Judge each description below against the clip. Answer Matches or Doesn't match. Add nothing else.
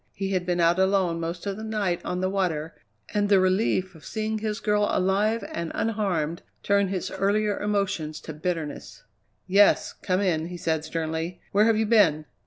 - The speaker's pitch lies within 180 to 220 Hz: Matches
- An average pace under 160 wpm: Doesn't match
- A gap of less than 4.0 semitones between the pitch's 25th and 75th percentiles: Matches